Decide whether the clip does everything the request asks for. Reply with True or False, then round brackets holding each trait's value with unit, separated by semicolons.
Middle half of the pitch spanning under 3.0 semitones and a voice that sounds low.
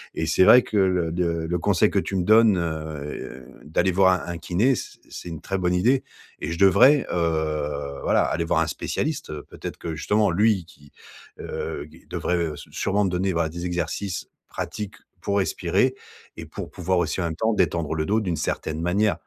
False (3.4 semitones; 90 Hz)